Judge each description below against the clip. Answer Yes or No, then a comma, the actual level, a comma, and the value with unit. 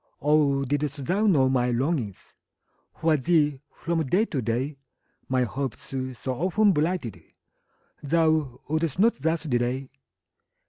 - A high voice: No, medium, 145 Hz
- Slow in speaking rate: Yes, slow, 125 wpm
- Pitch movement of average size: Yes, average, 3.9 semitones